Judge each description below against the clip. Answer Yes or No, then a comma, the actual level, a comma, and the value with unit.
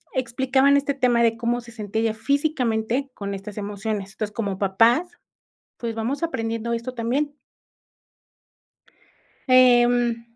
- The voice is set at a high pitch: Yes, high, 235 Hz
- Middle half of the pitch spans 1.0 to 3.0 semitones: Yes, narrow, 2.6 semitones